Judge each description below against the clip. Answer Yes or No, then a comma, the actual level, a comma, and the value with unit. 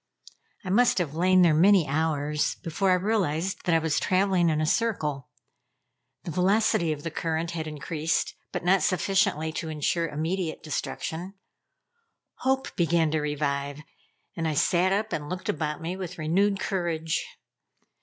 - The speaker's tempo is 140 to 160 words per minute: Yes, average, 155 wpm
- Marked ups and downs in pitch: No, average, 3.2 semitones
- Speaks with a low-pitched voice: No, medium, 165 Hz